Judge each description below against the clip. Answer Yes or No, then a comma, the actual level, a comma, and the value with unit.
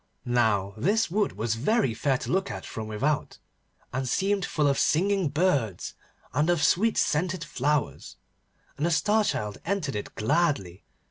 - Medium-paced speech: Yes, average, 155 wpm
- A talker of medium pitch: Yes, medium, 150 Hz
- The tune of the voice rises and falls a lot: Yes, wide, 8.0 semitones